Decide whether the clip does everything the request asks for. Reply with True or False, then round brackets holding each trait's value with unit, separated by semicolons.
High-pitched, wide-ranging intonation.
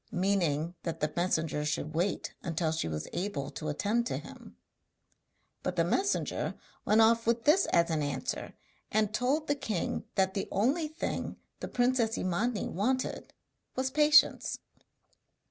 True (205 Hz; 7.1 semitones)